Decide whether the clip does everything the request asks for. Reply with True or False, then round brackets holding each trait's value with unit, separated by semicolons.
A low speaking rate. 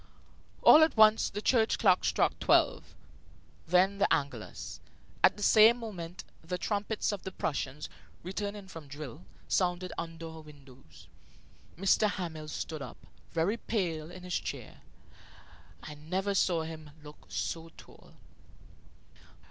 True (130 wpm)